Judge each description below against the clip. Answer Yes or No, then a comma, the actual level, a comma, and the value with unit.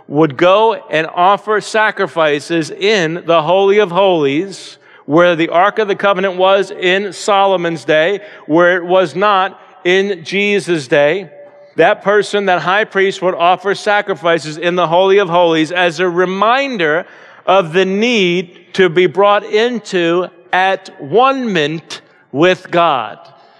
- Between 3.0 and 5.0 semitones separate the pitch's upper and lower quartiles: No, narrow, 2.4 semitones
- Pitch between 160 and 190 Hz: Yes, medium, 185 Hz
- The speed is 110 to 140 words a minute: Yes, slow, 135 wpm